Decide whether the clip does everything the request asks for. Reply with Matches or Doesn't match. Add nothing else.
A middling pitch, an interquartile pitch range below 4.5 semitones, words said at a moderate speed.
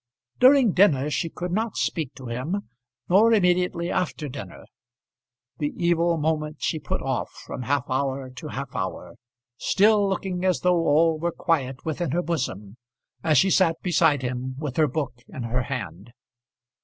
Doesn't match